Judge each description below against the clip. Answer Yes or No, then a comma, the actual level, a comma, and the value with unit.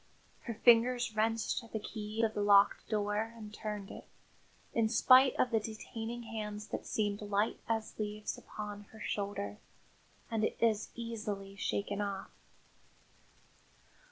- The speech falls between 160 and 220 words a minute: No, slow, 135 wpm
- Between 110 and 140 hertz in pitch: No, high, 215 Hz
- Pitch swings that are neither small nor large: No, narrow, 1.6 semitones